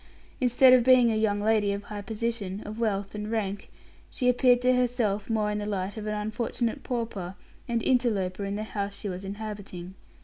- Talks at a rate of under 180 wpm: No, average, 195 wpm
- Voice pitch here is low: No, high, 215 Hz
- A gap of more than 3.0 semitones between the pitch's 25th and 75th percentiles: No, average, 2.7 semitones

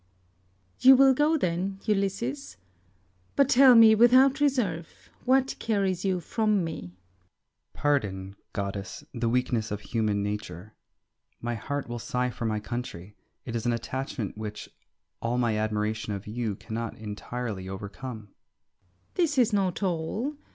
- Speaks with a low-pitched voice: Yes, low, 125 Hz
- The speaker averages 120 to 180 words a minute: Yes, average, 145 wpm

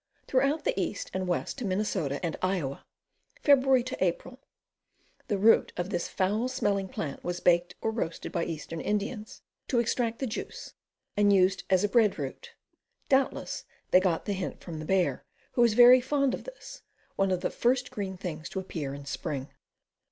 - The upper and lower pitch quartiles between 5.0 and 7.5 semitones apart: Yes, wide, 5.5 semitones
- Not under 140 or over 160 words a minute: No, average, 175 wpm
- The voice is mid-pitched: No, high, 200 Hz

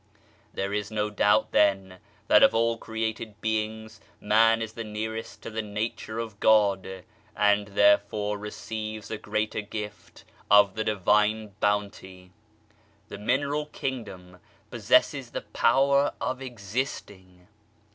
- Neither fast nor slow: No, slow, 125 wpm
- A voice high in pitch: No, low, 105 Hz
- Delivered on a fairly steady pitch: Yes, narrow, 1.5 semitones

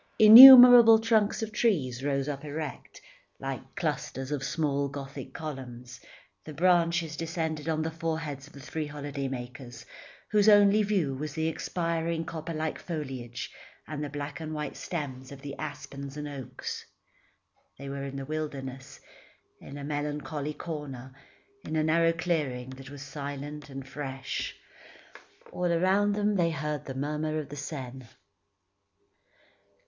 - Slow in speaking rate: No, average, 145 wpm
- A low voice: No, medium, 150 Hz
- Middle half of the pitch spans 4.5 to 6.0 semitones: No, average, 3.2 semitones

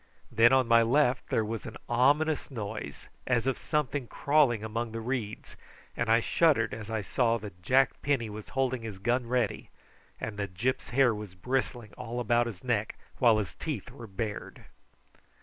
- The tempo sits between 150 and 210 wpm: Yes, average, 175 wpm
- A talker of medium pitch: No, low, 115 Hz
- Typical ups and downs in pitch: Yes, average, 3.0 semitones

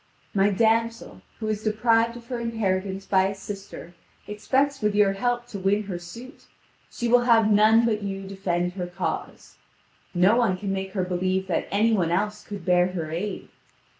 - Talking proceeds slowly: No, average, 180 wpm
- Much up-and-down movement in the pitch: No, average, 3.2 semitones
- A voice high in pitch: Yes, high, 200 Hz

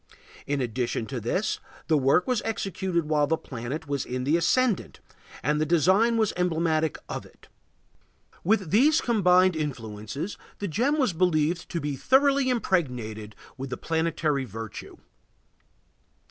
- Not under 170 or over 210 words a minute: No, average, 140 wpm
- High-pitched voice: No, medium, 160 Hz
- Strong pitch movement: Yes, wide, 6.2 semitones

